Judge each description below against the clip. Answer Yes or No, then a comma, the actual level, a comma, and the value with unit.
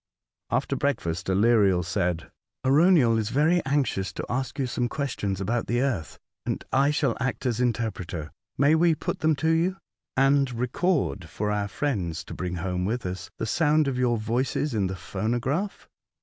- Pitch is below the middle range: Yes, low, 120 Hz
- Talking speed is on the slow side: No, average, 175 wpm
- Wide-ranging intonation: Yes, wide, 6.5 semitones